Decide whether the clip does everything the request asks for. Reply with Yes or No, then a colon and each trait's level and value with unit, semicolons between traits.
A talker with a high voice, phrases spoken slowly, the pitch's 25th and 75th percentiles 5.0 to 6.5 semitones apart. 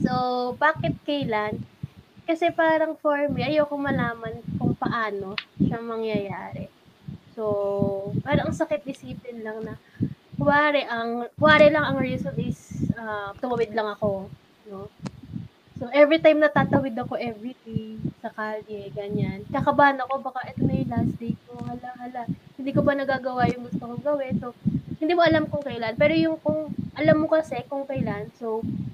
No: high, 245 Hz; fast, 155 wpm; average, 5.3 semitones